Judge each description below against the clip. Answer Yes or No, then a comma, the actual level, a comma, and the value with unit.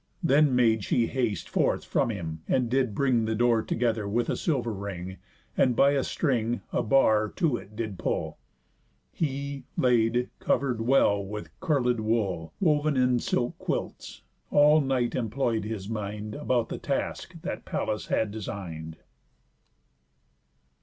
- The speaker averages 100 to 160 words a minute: Yes, average, 145 wpm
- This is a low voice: Yes, low, 115 Hz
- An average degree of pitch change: Yes, average, 3.8 semitones